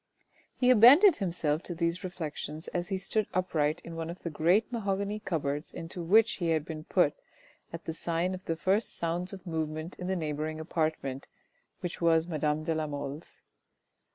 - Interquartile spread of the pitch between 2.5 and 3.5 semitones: Yes, average, 3.0 semitones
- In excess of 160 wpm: Yes, average, 180 wpm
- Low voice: No, medium, 170 Hz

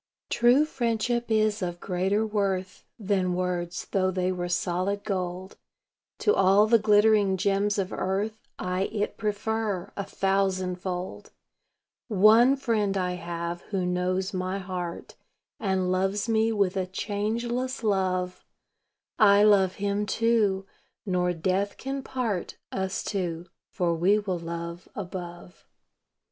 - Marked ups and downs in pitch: No, average, 2.7 semitones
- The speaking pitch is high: Yes, high, 195 Hz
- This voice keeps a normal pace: No, slow, 125 wpm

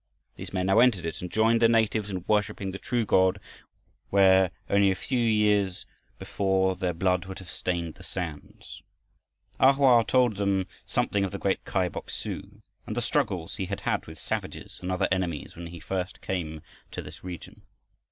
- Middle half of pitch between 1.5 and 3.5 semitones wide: Yes, narrow, 2.5 semitones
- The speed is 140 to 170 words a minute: No, average, 185 wpm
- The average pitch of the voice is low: Yes, very low, 95 Hz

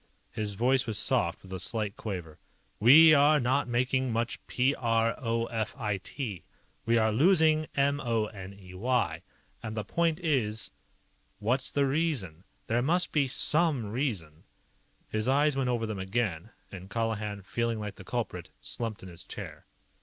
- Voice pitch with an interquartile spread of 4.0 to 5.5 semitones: Yes, average, 4.6 semitones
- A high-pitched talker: No, low, 115 Hz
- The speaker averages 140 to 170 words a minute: Yes, average, 165 wpm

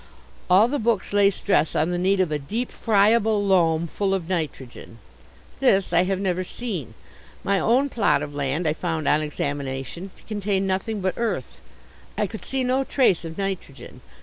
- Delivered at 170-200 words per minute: Yes, average, 175 wpm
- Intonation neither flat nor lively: Yes, average, 4.6 semitones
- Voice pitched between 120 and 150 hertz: No, high, 190 Hz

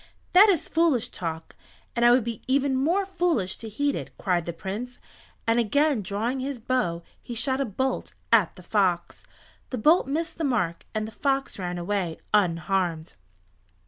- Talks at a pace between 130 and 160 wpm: No, average, 175 wpm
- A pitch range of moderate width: No, wide, 6.6 semitones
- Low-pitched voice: No, high, 235 Hz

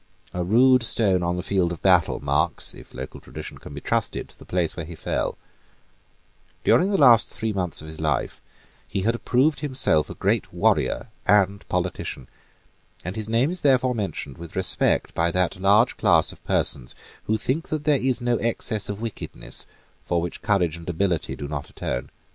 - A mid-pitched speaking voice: No, low, 100 Hz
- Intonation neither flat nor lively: No, wide, 5.9 semitones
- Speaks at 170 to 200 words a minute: Yes, average, 185 wpm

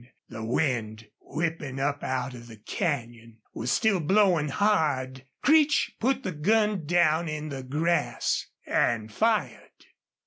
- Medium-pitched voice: Yes, medium, 150 Hz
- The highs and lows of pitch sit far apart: Yes, wide, 6.6 semitones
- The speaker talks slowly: Yes, slow, 130 wpm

